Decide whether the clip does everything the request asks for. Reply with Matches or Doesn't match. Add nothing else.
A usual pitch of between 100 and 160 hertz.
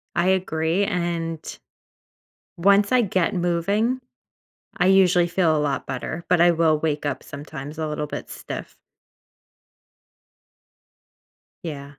Doesn't match